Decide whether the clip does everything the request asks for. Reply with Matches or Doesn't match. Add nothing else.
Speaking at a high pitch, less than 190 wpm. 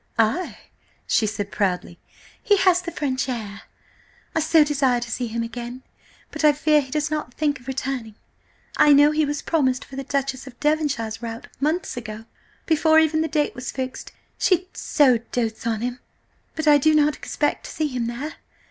Matches